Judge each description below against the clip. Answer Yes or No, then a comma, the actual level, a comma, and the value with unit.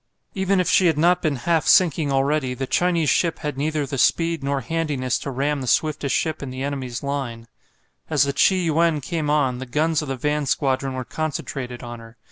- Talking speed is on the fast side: Yes, fast, 210 wpm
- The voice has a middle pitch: Yes, medium, 145 Hz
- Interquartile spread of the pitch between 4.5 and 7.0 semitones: No, average, 3.3 semitones